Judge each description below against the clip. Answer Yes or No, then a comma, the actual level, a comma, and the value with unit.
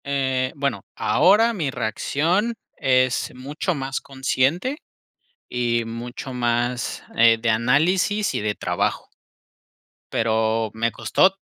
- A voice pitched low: Yes, low, 130 Hz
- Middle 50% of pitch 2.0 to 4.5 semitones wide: No, average, 5.2 semitones